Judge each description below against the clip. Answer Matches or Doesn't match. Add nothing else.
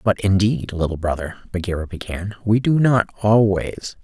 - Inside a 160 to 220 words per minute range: Doesn't match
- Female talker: Doesn't match